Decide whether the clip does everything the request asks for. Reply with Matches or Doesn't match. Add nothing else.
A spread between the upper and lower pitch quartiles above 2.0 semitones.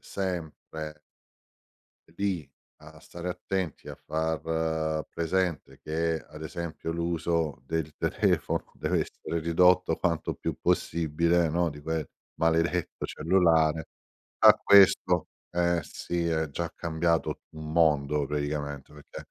Doesn't match